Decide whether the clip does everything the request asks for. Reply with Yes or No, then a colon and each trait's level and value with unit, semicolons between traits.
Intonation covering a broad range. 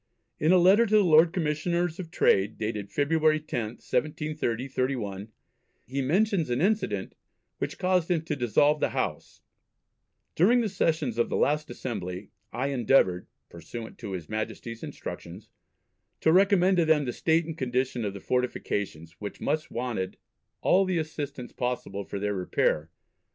Yes: wide, 7.0 semitones